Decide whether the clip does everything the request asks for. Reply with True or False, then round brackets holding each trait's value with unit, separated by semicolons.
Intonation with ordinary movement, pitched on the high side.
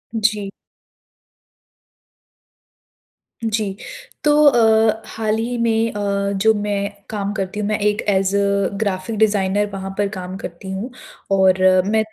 False (2.0 semitones; 205 Hz)